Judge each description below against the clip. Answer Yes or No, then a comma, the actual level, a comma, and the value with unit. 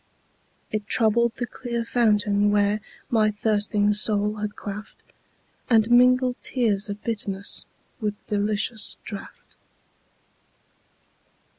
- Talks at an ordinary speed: No, slow, 100 wpm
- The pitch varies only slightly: Yes, narrow, 2.1 semitones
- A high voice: Yes, high, 210 Hz